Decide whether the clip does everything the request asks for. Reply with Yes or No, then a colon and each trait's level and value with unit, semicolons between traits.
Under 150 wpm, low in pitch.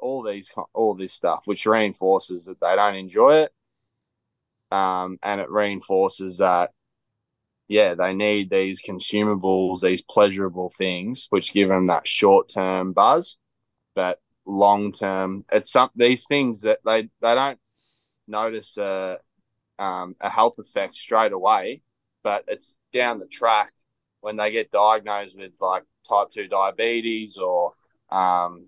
Yes: average, 140 wpm; low, 100 Hz